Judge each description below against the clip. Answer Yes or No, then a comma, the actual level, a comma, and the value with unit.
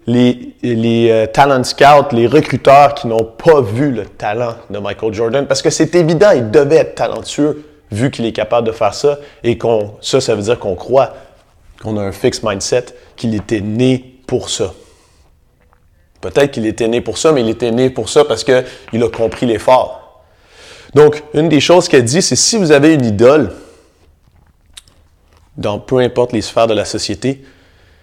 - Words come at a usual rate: Yes, average, 185 wpm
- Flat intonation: No, average, 4.7 semitones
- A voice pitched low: Yes, low, 120 Hz